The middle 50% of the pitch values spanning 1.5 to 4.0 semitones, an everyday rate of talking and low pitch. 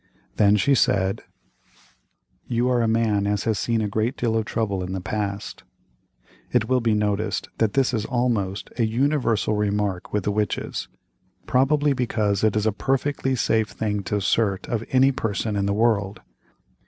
Yes: average, 2.8 semitones; average, 170 wpm; low, 110 Hz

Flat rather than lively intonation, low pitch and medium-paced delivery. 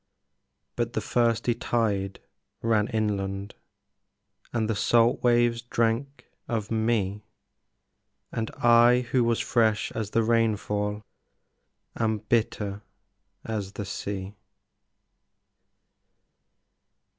No: narrow, 2.1 semitones; low, 110 Hz; slow, 90 wpm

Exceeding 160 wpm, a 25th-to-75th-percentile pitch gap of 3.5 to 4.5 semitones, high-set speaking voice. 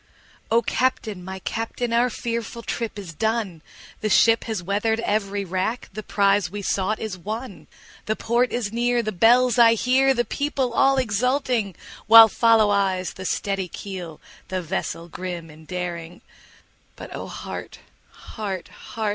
No: average, 155 wpm; average, 3.8 semitones; high, 215 Hz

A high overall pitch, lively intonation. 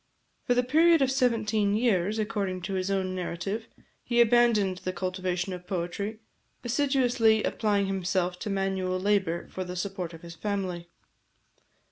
No: high, 195 Hz; average, 3.5 semitones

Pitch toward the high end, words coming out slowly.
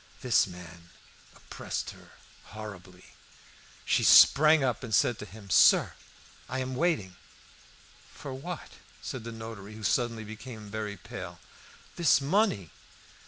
No: low, 110 Hz; slow, 125 wpm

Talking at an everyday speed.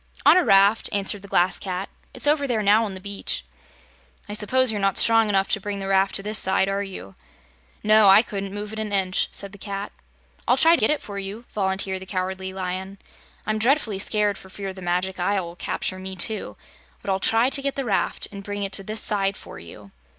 No: fast, 230 wpm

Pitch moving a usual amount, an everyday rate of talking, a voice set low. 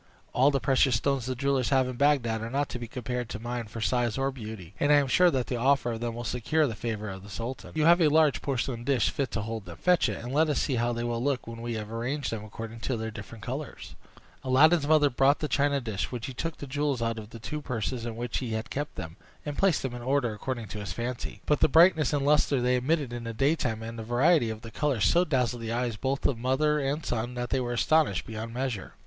No: average, 3.7 semitones; fast, 265 wpm; low, 125 Hz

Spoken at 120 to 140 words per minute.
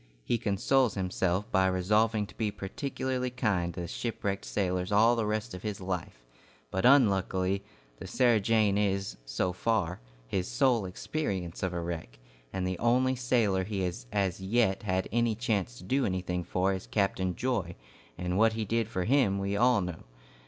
No: average, 175 wpm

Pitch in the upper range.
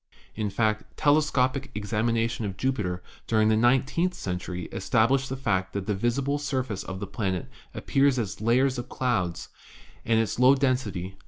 No: low, 115 Hz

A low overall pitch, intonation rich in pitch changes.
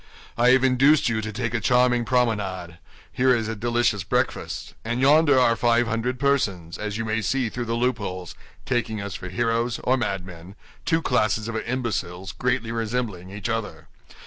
No: low, 115 Hz; average, 3.1 semitones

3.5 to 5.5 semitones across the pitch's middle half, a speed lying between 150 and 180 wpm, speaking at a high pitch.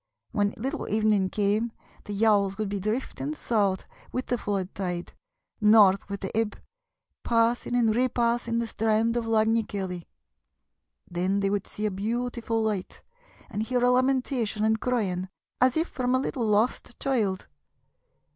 No: average, 3.1 semitones; average, 155 wpm; high, 220 Hz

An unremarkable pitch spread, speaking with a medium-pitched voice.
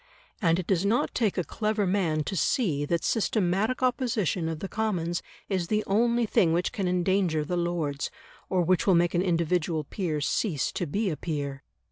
Yes: average, 3.9 semitones; medium, 180 Hz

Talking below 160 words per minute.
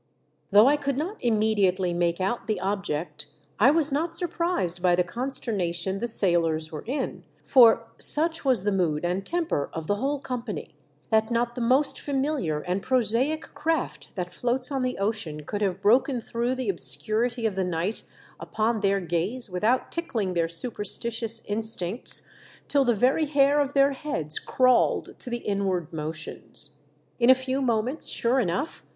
No: average, 170 wpm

